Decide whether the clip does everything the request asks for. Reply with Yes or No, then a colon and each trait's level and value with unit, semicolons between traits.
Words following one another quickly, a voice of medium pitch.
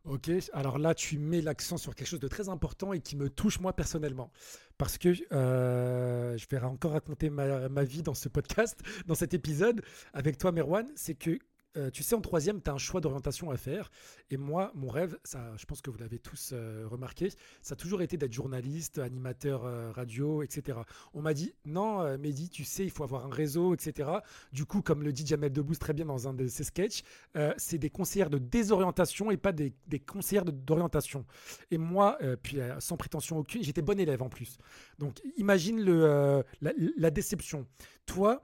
No: average, 210 wpm; medium, 150 Hz